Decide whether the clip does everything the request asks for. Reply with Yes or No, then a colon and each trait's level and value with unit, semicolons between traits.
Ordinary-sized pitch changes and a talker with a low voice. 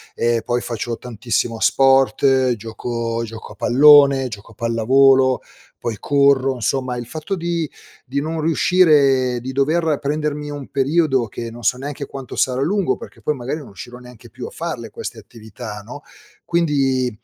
Yes: average, 3.5 semitones; low, 130 Hz